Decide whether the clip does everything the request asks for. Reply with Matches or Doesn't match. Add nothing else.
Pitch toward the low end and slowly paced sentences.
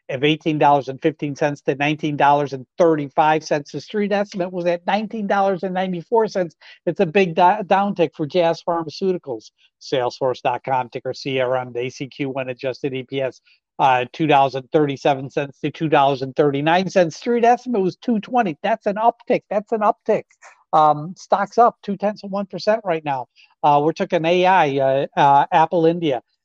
Doesn't match